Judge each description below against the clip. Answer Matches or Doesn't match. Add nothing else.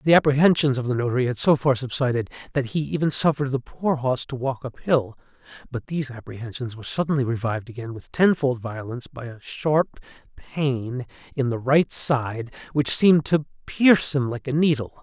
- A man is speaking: Matches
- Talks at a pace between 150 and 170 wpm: Doesn't match